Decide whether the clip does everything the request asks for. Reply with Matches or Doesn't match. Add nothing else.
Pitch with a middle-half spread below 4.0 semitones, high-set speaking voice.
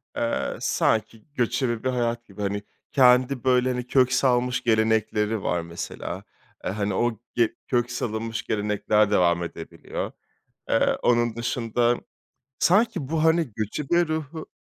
Doesn't match